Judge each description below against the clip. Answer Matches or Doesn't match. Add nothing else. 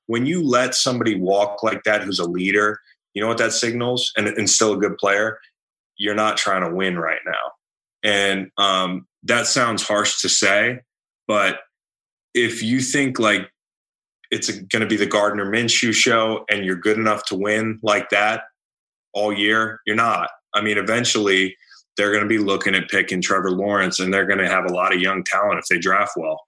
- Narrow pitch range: Matches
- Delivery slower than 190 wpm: Doesn't match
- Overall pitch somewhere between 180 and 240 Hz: Doesn't match